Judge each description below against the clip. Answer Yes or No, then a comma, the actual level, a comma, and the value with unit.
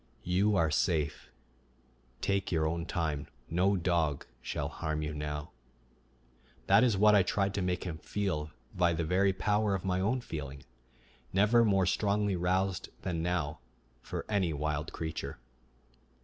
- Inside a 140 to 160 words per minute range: Yes, average, 150 wpm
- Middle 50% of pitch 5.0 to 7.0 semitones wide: No, average, 3.9 semitones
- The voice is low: Yes, very low, 90 Hz